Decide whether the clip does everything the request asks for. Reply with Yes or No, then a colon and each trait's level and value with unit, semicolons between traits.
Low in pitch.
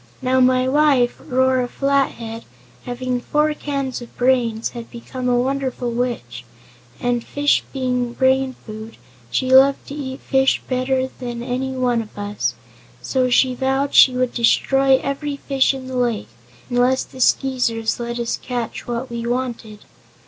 No: very high, 255 Hz